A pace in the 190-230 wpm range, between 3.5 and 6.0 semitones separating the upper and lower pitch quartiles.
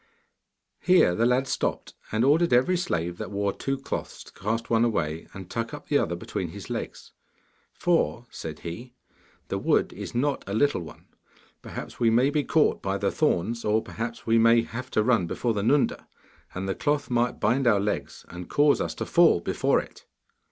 Yes: average, 195 wpm; average, 5.3 semitones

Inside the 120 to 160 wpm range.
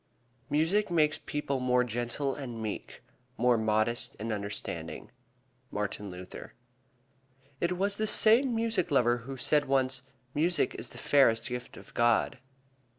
Yes: slow, 135 wpm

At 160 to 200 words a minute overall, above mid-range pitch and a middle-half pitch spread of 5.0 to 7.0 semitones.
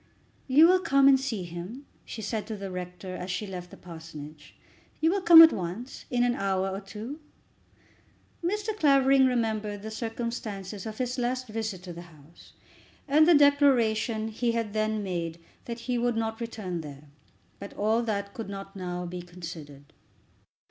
Yes: average, 170 wpm; high, 215 Hz; wide, 5.4 semitones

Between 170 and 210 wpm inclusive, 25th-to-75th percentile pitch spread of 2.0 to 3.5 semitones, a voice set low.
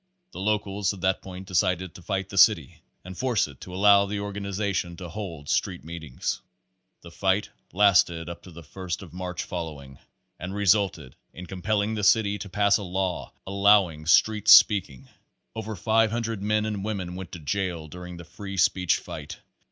Yes: average, 175 wpm; average, 2.8 semitones; very low, 95 Hz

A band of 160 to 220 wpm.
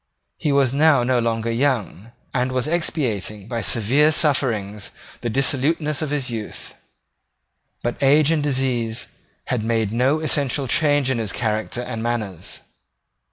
No: average, 140 wpm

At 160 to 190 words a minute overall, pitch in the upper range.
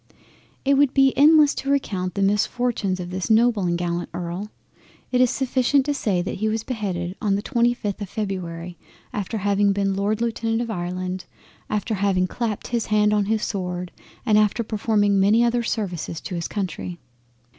Yes: average, 175 wpm; high, 205 Hz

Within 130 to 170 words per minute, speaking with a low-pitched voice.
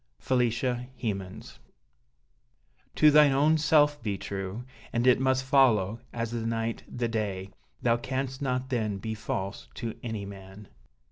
Yes: average, 140 wpm; low, 115 Hz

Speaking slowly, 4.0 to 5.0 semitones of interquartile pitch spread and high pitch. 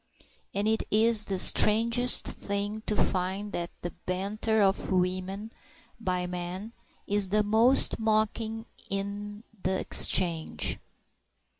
No: slow, 115 wpm; average, 2.7 semitones; high, 205 Hz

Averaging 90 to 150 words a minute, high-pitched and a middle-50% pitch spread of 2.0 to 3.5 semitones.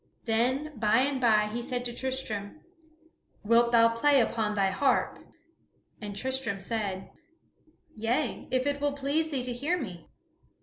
No: average, 145 wpm; high, 240 Hz; average, 4.0 semitones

